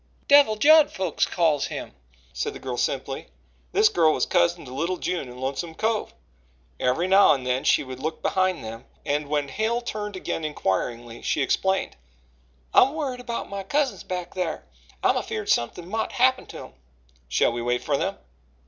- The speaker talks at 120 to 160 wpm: No, average, 175 wpm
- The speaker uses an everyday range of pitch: No, wide, 8.4 semitones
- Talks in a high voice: No, medium, 170 Hz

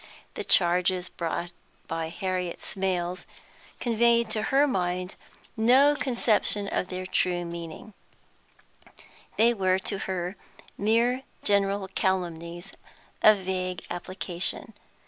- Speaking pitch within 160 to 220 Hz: Yes, high, 190 Hz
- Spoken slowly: Yes, slow, 105 wpm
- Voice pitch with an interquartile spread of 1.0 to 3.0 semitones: No, average, 3.4 semitones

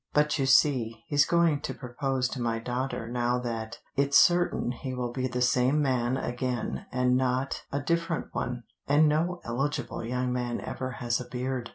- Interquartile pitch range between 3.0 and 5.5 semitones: No, narrow, 2.5 semitones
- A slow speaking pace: No, average, 180 wpm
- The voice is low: Yes, low, 125 Hz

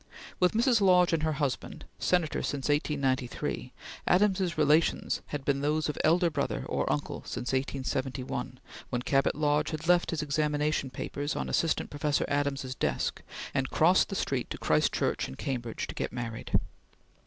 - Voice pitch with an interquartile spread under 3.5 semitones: Yes, average, 3.0 semitones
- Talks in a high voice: No, medium, 145 Hz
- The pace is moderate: Yes, average, 160 wpm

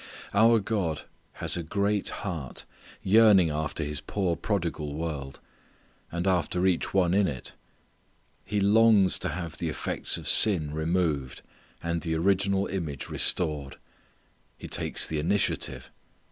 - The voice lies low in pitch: Yes, very low, 85 Hz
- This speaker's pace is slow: Yes, slow, 130 wpm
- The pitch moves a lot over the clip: No, average, 4.1 semitones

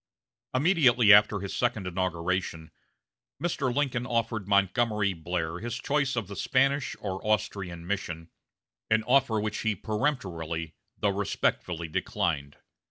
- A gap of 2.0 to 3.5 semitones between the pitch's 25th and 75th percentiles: No, average, 5.2 semitones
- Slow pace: Yes, slow, 125 wpm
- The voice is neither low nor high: No, low, 105 Hz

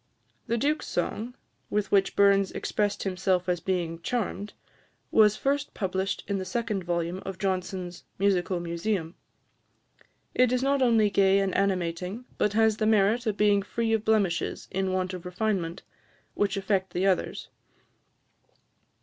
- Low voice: No, high, 195 Hz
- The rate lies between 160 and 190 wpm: No, average, 145 wpm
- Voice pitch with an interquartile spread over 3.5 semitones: No, average, 2.9 semitones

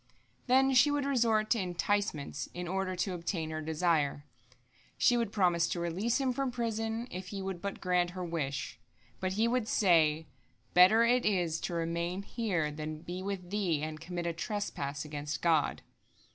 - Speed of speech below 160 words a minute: No, average, 175 wpm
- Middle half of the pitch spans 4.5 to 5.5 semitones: Yes, average, 4.8 semitones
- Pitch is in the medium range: Yes, medium, 180 Hz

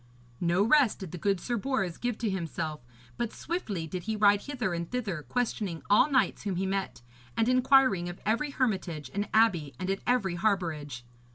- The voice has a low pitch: No, high, 200 Hz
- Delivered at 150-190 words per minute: Yes, average, 185 wpm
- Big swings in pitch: Yes, wide, 5.7 semitones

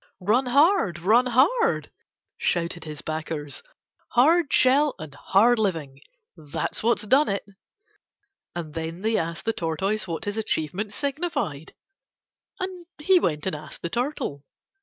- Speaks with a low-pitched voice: No, high, 205 Hz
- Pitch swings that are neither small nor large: No, wide, 8.2 semitones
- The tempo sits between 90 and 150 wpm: Yes, average, 140 wpm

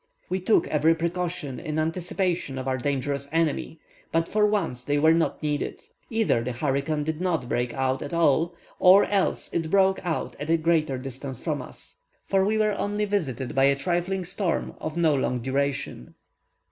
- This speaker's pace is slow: No, average, 180 wpm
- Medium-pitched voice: Yes, medium, 160 Hz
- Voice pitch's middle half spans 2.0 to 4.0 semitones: No, average, 4.6 semitones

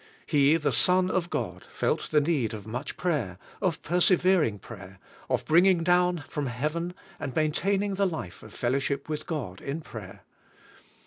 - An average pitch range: No, wide, 6.4 semitones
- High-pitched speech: No, medium, 155 Hz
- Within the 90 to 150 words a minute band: No, average, 165 wpm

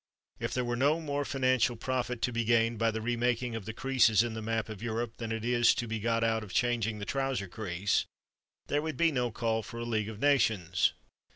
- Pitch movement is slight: Yes, narrow, 2.0 semitones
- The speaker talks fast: Yes, fast, 220 wpm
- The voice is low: Yes, low, 115 Hz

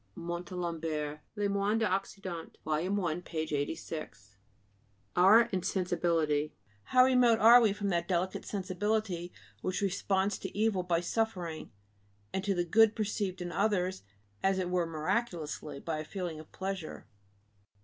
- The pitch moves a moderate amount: Yes, average, 3.4 semitones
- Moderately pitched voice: Yes, medium, 180 Hz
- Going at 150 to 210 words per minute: No, slow, 135 wpm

